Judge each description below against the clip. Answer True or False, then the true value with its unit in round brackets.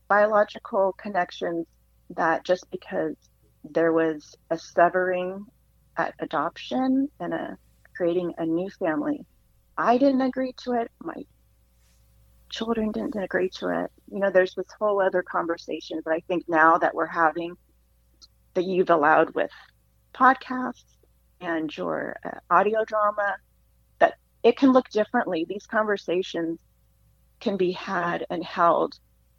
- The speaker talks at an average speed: False (130 wpm)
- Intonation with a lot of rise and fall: False (4.7 semitones)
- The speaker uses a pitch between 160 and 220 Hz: True (185 Hz)